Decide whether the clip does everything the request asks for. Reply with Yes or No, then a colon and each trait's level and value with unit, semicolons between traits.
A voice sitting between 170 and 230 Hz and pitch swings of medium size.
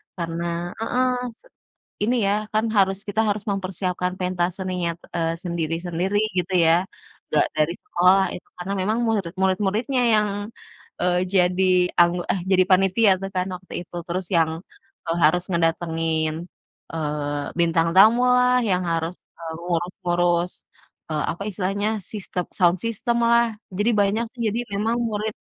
Yes: medium, 185 Hz; average, 3.2 semitones